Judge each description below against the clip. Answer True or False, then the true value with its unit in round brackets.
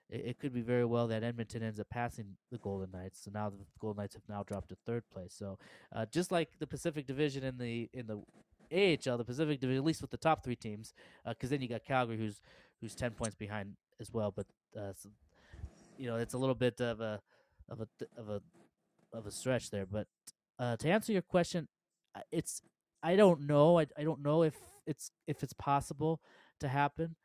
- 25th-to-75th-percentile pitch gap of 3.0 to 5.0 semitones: False (5.4 semitones)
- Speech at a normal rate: False (220 wpm)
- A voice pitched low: True (120 Hz)